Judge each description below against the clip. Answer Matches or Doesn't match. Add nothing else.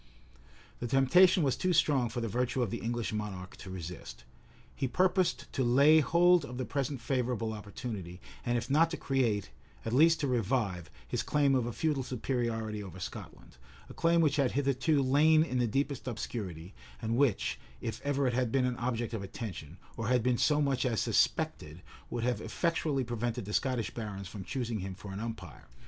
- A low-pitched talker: Matches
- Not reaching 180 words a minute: Doesn't match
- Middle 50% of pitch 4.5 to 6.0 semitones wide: Doesn't match